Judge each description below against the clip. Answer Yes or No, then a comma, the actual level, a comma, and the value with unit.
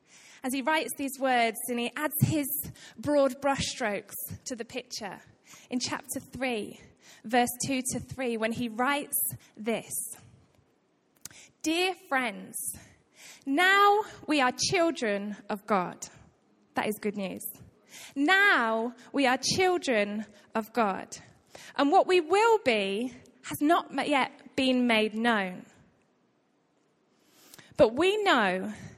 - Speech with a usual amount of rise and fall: Yes, average, 4.7 semitones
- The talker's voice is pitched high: Yes, very high, 255 Hz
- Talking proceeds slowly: Yes, slow, 120 wpm